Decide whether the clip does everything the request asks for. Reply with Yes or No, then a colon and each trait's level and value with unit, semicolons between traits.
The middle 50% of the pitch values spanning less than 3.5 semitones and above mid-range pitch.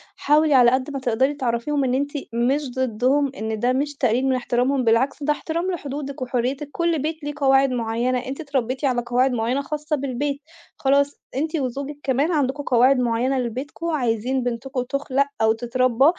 Yes: narrow, 2.6 semitones; very high, 265 Hz